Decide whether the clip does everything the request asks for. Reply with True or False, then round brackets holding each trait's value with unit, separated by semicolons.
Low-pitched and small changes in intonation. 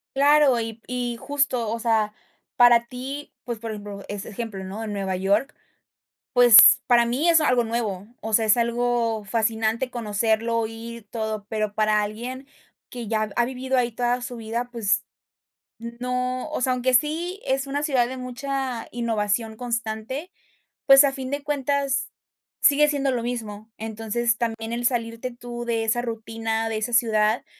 False (235 Hz; 2.3 semitones)